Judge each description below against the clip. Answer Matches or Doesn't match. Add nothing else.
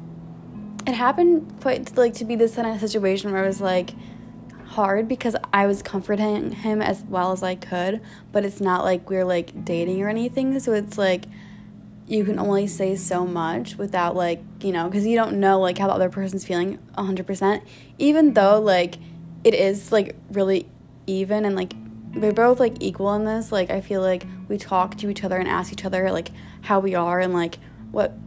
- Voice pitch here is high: Matches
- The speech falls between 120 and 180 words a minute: Doesn't match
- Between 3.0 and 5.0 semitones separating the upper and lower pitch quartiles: Doesn't match